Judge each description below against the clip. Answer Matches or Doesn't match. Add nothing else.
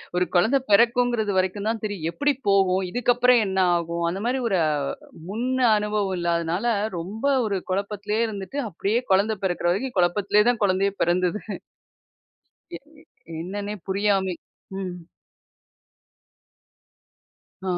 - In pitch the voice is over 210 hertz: Doesn't match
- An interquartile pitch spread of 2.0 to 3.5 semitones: Matches